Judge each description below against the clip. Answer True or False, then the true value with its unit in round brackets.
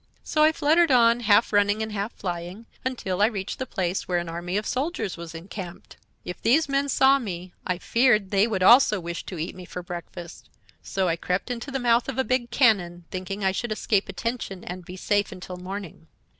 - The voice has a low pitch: False (200 Hz)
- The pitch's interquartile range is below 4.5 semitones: False (4.9 semitones)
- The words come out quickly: True (210 wpm)